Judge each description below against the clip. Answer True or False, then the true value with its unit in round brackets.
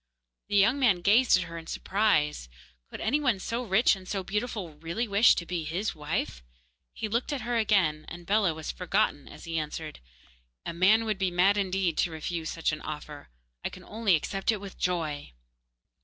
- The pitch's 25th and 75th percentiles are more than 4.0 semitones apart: True (4.6 semitones)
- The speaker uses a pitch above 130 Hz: True (190 Hz)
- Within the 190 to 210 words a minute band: True (195 wpm)